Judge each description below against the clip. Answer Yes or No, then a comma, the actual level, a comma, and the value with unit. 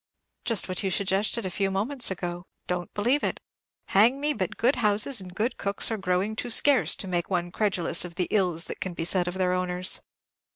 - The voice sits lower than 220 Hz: Yes, high, 190 Hz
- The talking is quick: Yes, fast, 210 wpm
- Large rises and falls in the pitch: No, average, 3.2 semitones